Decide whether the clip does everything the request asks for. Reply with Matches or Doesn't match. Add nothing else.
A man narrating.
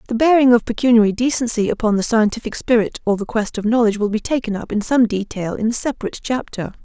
Doesn't match